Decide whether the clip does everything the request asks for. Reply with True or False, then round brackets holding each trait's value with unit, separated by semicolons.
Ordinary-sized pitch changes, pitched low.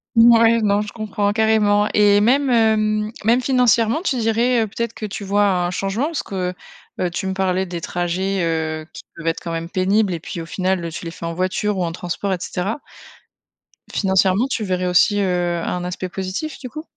False (3.6 semitones; 200 Hz)